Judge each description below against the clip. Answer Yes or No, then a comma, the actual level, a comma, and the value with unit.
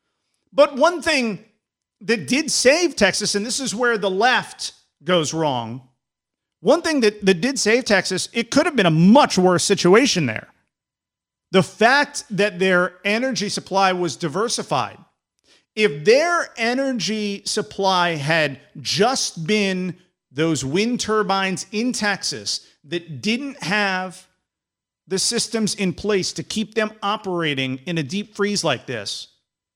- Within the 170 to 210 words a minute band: No, slow, 135 wpm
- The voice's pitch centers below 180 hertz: No, high, 200 Hz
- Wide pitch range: No, average, 4.3 semitones